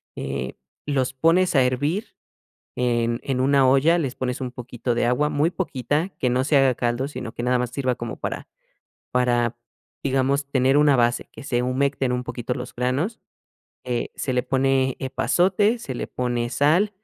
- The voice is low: Yes, low, 130 Hz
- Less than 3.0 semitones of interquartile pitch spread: Yes, narrow, 2.5 semitones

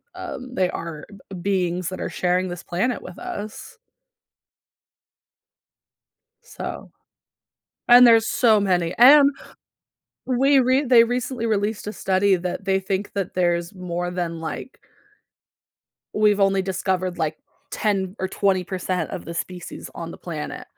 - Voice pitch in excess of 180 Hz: Yes, high, 190 Hz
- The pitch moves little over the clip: No, average, 4.0 semitones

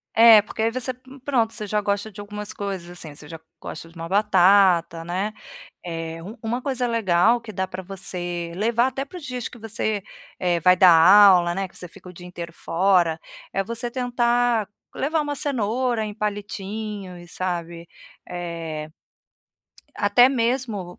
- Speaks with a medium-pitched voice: No, high, 200 Hz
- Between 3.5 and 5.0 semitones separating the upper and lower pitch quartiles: Yes, average, 4.7 semitones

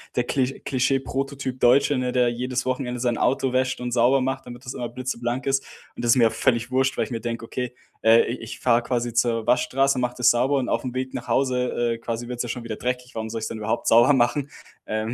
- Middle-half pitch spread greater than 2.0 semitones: No, narrow, 1.6 semitones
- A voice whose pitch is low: Yes, low, 125 Hz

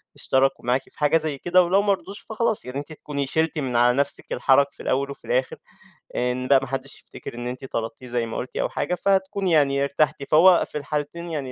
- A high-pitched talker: No, medium, 140 Hz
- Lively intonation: No, average, 4.6 semitones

